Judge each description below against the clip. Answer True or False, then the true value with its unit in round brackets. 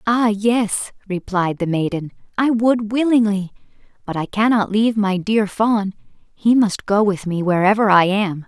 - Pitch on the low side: False (205 Hz)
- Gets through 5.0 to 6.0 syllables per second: False (4.4 syllables/s)